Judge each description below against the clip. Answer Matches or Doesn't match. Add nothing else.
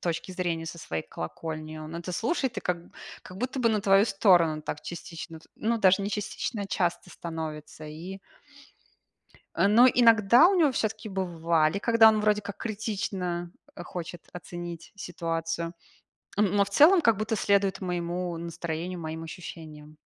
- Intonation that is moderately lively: Matches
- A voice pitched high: Doesn't match